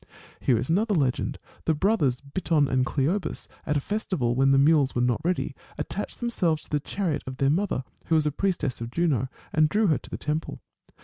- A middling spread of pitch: Yes, average, 5.0 semitones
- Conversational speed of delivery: No, fast, 210 wpm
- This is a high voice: No, medium, 150 Hz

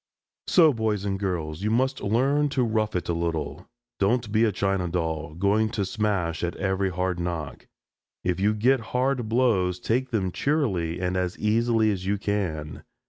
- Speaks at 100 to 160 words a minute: No, average, 175 wpm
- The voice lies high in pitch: No, low, 100 Hz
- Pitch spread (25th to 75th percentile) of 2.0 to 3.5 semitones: No, average, 4.1 semitones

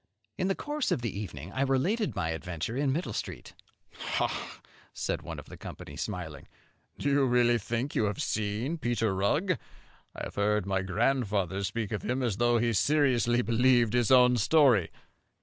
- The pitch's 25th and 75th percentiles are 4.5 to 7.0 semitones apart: Yes, average, 4.8 semitones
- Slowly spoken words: No, average, 175 wpm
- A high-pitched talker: No, low, 120 Hz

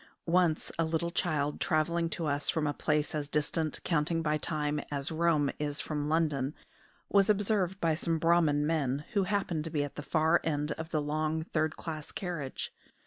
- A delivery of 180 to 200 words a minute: Yes, average, 185 wpm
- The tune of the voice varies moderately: No, narrow, 2.1 semitones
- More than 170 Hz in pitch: No, medium, 155 Hz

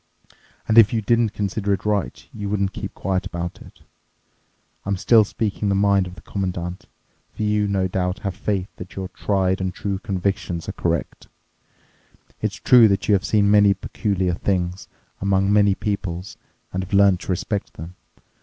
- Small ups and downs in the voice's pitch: Yes, narrow, 1.8 semitones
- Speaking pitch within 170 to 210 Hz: No, low, 100 Hz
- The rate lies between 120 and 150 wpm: No, average, 165 wpm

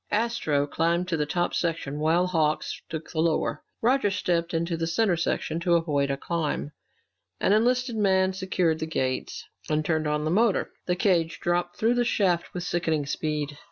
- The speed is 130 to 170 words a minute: No, average, 180 wpm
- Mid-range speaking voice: Yes, medium, 170 Hz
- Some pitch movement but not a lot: Yes, average, 3.2 semitones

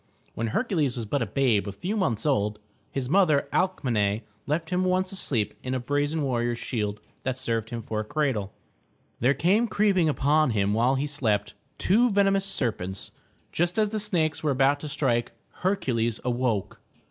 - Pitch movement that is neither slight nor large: No, wide, 7.4 semitones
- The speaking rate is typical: Yes, average, 175 wpm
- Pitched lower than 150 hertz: Yes, low, 135 Hz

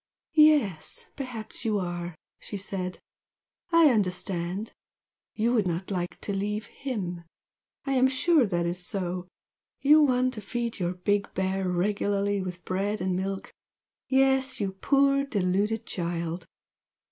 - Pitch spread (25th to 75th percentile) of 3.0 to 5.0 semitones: No, wide, 5.5 semitones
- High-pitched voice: Yes, high, 200 Hz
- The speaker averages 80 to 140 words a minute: Yes, slow, 135 wpm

